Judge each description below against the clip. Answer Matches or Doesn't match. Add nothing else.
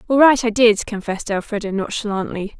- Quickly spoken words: Doesn't match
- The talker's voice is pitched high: Matches